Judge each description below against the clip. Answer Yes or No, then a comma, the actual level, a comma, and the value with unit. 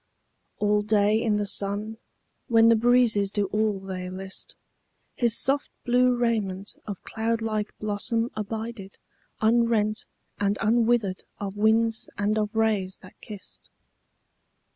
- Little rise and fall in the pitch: Yes, narrow, 2.1 semitones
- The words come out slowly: Yes, slow, 120 wpm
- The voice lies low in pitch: No, high, 215 Hz